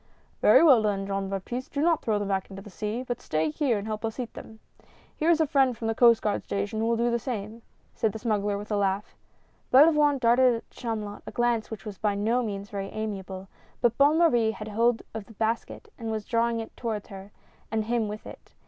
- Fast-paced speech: Yes, fast, 230 wpm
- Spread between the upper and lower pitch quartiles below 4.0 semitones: Yes, average, 2.7 semitones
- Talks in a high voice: Yes, high, 220 Hz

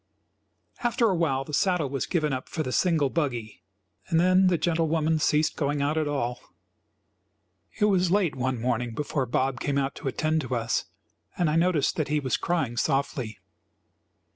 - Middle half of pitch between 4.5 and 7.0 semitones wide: No, average, 4.1 semitones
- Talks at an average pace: Yes, average, 175 wpm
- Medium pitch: Yes, medium, 150 Hz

